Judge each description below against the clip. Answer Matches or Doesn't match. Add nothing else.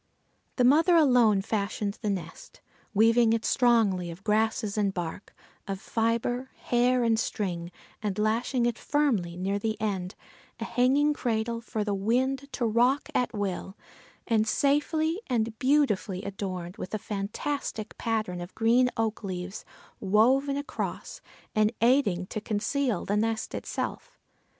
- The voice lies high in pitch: Matches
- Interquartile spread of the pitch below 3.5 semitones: Doesn't match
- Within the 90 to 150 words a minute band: Matches